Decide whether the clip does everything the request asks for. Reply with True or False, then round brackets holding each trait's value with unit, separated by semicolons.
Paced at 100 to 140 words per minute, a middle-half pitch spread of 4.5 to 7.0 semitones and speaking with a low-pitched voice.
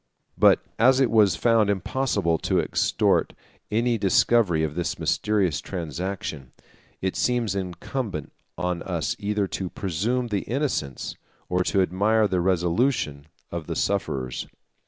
True (135 wpm; 4.8 semitones; 95 Hz)